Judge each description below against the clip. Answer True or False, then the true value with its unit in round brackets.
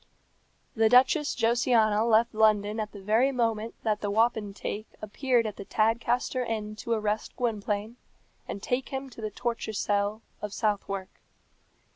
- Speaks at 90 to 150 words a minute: True (145 wpm)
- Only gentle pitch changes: True (2.1 semitones)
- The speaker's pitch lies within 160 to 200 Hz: False (220 Hz)